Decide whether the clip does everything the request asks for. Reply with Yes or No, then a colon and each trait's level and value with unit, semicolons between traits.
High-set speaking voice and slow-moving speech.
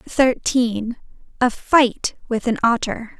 Yes: high, 240 Hz; slow, 115 wpm